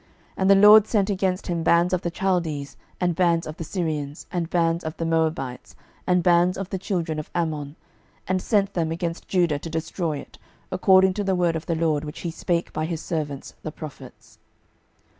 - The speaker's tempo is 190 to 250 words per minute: Yes, average, 200 wpm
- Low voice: No, medium, 170 Hz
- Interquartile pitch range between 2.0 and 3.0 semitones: Yes, narrow, 2.6 semitones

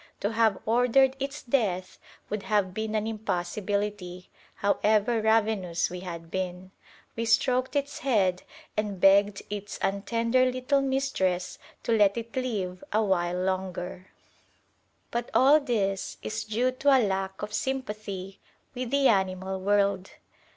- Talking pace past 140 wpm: No, slow, 135 wpm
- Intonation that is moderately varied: Yes, average, 3.9 semitones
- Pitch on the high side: Yes, high, 210 Hz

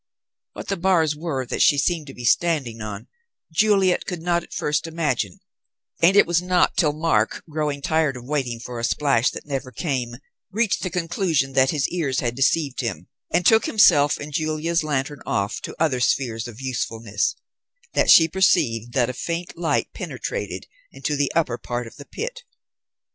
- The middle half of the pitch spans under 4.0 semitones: No, average, 5.2 semitones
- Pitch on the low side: No, medium, 145 Hz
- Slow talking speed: No, average, 180 wpm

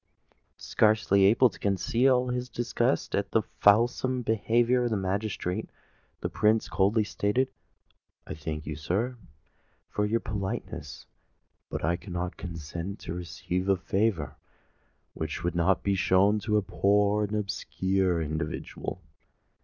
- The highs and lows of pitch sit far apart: No, average, 3.7 semitones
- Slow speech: Yes, slow, 130 wpm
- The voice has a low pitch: Yes, low, 100 Hz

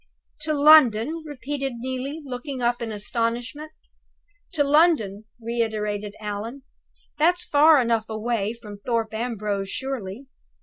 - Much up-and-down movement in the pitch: No, average, 4.7 semitones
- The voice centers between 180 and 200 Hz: No, high, 240 Hz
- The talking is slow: Yes, slow, 115 wpm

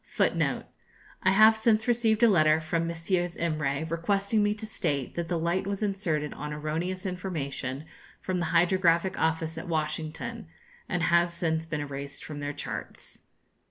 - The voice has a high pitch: No, medium, 170 Hz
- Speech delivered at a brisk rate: No, average, 160 wpm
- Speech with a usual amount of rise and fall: Yes, average, 3.7 semitones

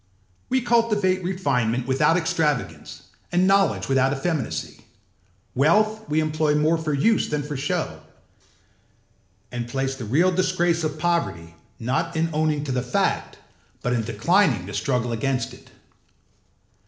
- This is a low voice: No, medium, 150 Hz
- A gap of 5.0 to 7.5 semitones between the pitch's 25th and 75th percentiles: Yes, wide, 5.6 semitones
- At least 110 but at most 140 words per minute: Yes, slow, 135 wpm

